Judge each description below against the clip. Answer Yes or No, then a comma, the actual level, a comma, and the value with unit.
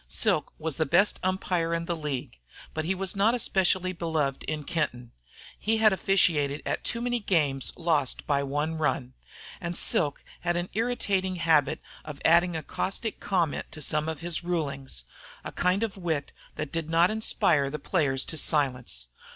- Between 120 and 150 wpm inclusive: No, average, 170 wpm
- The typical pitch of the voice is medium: Yes, medium, 165 Hz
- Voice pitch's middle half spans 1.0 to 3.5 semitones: No, average, 4.2 semitones